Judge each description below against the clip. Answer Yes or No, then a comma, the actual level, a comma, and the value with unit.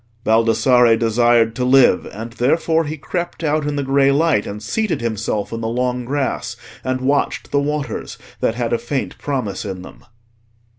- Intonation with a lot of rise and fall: No, average, 4.0 semitones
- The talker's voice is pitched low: Yes, low, 125 Hz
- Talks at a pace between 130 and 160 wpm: No, average, 170 wpm